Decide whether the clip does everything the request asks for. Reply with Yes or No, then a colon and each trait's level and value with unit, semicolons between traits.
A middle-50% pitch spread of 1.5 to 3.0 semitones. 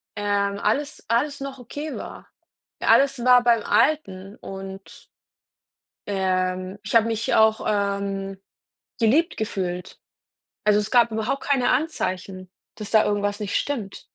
No: average, 3.9 semitones